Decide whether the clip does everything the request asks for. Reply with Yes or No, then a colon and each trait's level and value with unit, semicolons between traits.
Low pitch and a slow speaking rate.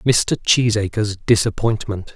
Yes: low, 105 Hz; slow, 85 wpm